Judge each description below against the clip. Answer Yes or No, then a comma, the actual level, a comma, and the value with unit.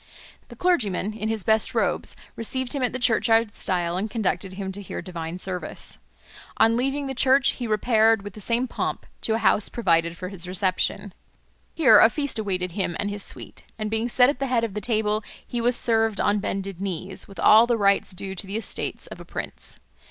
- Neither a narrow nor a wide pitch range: Yes, average, 3.5 semitones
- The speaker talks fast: Yes, fast, 210 wpm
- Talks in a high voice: Yes, high, 215 Hz